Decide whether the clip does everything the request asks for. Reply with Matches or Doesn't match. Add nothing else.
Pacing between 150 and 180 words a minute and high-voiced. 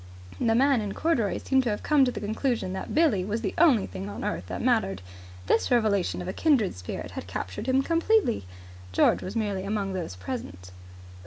Doesn't match